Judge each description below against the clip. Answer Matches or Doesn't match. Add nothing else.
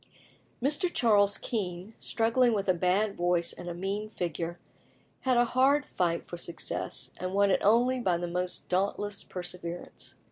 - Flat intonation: Doesn't match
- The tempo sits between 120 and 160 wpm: Matches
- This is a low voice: Doesn't match